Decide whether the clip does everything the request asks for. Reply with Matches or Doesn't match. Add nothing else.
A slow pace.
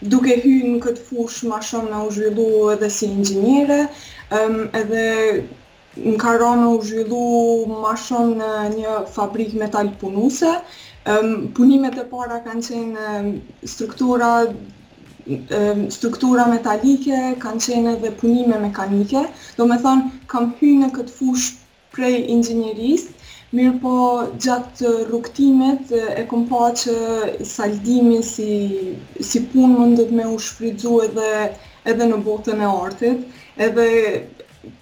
Matches